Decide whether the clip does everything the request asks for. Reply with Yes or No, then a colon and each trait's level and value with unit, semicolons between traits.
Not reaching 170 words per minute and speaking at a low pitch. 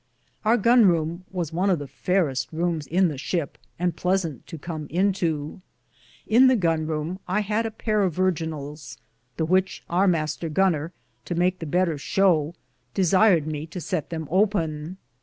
No: average, 160 wpm; medium, 170 Hz